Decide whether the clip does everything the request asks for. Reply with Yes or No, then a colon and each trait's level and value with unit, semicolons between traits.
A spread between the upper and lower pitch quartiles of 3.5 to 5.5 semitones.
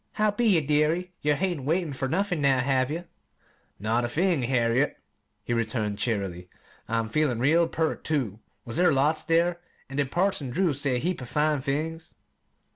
Yes: average, 5.2 semitones